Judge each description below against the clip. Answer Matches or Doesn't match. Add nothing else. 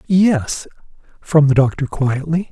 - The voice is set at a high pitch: Doesn't match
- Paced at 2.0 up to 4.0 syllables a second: Matches